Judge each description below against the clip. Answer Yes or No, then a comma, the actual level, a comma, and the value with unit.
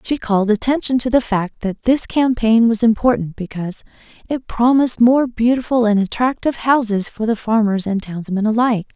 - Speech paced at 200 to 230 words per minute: No, average, 170 wpm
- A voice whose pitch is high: Yes, high, 225 Hz